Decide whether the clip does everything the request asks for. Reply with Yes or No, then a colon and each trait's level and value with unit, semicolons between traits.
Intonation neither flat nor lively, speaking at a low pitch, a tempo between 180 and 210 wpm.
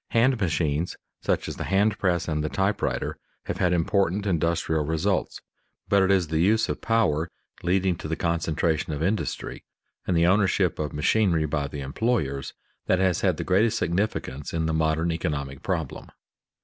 No: average, 3.7 semitones; very low, 85 Hz; average, 170 wpm